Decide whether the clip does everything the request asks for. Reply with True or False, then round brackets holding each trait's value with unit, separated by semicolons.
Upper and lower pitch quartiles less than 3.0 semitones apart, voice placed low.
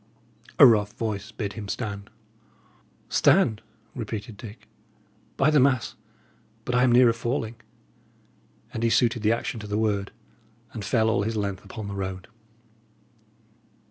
True (2.6 semitones; 110 Hz)